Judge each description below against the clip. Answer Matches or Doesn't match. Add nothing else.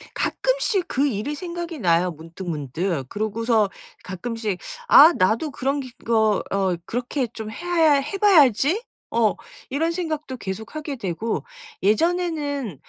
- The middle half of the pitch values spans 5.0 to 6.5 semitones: Doesn't match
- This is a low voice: Doesn't match